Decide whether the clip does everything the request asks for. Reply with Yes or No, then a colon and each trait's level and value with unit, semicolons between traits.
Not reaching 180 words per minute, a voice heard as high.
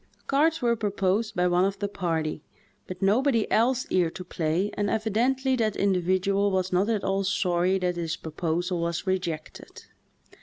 Yes: average, 160 wpm; high, 195 Hz